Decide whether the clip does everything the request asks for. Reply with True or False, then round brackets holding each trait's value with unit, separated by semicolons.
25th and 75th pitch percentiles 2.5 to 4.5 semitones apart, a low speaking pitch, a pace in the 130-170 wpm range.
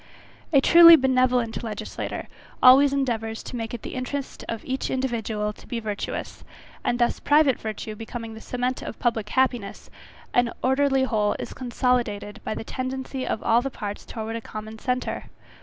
False (2.9 semitones; 245 Hz; 165 wpm)